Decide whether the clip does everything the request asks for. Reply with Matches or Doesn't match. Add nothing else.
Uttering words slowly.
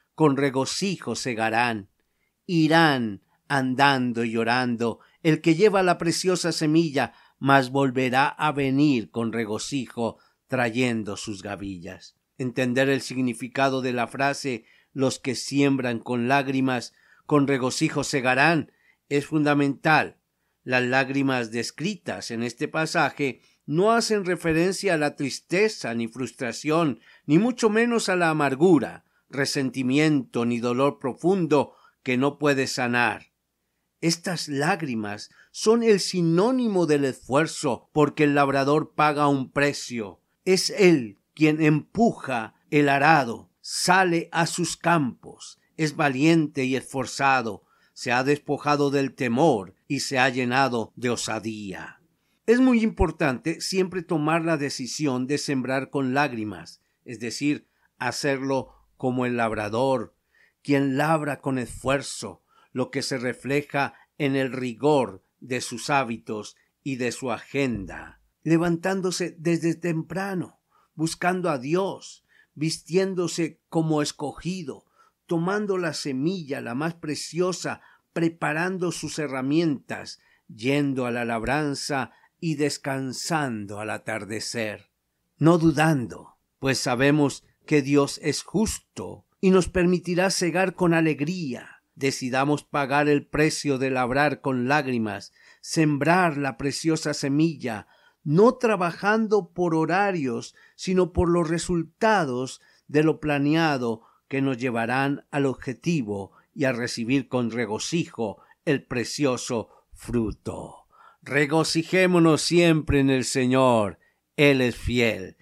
Matches